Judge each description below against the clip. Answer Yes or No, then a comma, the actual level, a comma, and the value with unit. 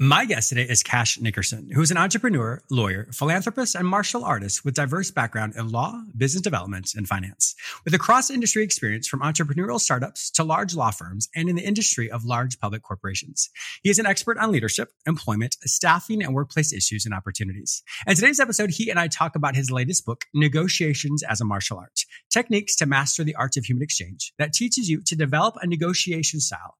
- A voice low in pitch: No, medium, 145 Hz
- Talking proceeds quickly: No, average, 195 wpm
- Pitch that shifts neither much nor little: No, wide, 7.8 semitones